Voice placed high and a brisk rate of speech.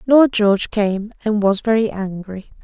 No: high, 210 Hz; average, 160 wpm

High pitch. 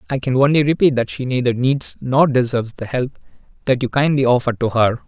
No: low, 130 Hz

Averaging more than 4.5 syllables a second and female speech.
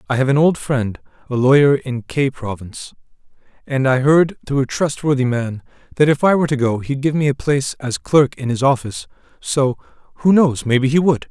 No: 5.5 syllables/s; male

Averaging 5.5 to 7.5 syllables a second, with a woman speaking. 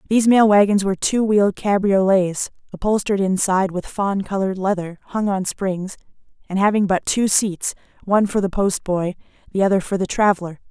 Yes: 5.6 syllables/s; female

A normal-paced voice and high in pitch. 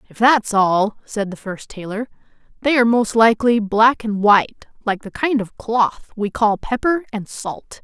Yes: average, 185 wpm; high, 220 Hz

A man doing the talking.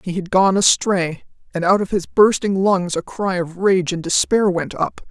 No: female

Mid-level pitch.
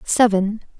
No: high, 210 Hz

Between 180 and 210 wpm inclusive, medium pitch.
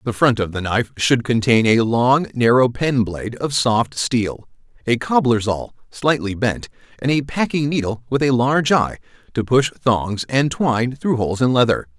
No: average, 185 wpm; low, 120 Hz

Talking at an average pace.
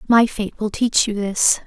No: fast, 215 wpm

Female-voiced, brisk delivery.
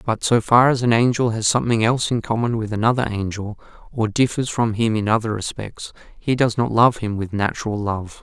No: male; fast, 210 wpm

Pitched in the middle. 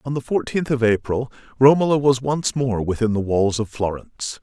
No: low, 125 Hz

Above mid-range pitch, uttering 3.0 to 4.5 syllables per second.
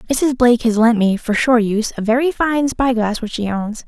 No: high, 235 Hz; 5.5 syllables/s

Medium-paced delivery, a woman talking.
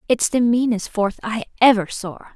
Yes: average, 180 wpm; female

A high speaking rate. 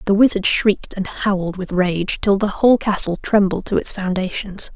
No: average, 190 wpm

